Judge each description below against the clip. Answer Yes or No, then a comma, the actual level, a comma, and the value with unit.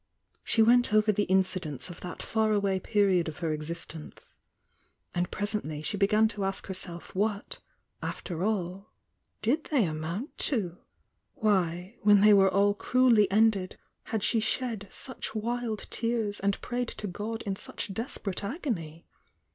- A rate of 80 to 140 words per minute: No, average, 150 wpm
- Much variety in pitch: No, average, 3.4 semitones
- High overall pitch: Yes, high, 205 Hz